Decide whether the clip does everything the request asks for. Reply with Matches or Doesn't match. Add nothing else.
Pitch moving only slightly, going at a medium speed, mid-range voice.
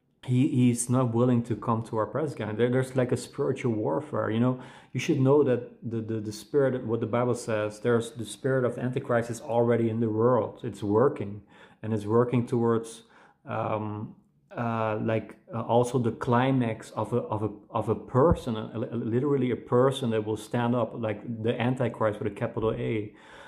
Doesn't match